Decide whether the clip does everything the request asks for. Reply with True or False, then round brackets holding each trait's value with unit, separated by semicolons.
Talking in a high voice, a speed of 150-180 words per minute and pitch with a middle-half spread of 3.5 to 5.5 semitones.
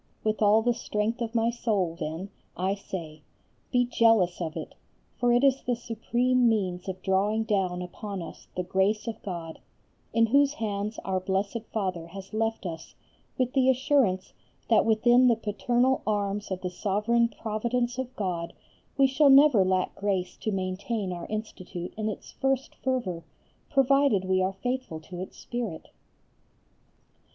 True (215 Hz; 160 wpm; 4.3 semitones)